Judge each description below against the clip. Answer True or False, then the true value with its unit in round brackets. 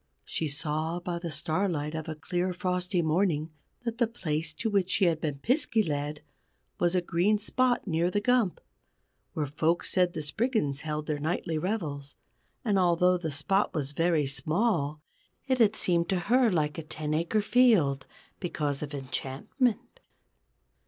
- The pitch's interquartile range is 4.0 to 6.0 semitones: True (4.9 semitones)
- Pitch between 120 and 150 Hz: False (170 Hz)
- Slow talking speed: False (160 wpm)